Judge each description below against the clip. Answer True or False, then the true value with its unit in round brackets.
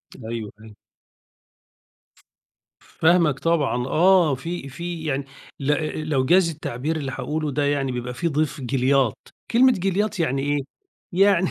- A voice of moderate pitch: True (145 Hz)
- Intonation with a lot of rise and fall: False (4.4 semitones)